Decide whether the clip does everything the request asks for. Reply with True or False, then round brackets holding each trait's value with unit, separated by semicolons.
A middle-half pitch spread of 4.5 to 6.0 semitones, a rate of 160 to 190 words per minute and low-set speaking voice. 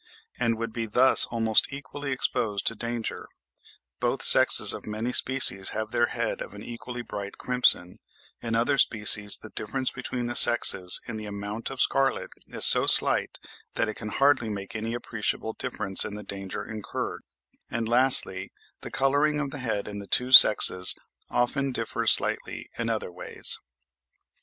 False (3.2 semitones; 165 wpm; 115 Hz)